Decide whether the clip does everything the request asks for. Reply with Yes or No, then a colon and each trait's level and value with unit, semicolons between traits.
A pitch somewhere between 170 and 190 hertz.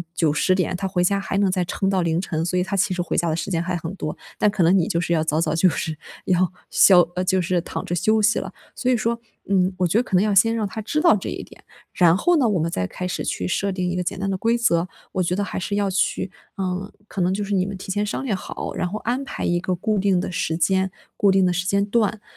Yes: medium, 185 Hz